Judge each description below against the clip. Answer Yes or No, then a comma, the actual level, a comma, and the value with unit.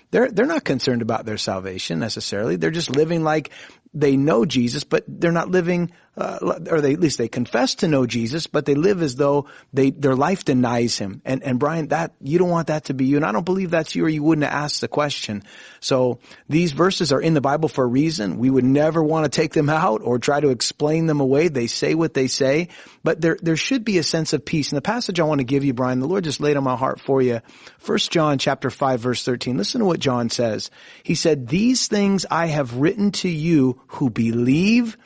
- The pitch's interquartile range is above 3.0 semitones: Yes, average, 4.1 semitones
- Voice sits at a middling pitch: Yes, medium, 150 Hz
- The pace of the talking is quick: Yes, fast, 240 wpm